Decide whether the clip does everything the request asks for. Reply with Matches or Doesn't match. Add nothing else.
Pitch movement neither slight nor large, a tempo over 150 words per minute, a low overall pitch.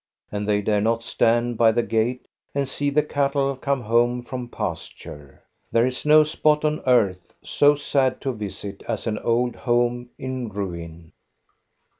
Matches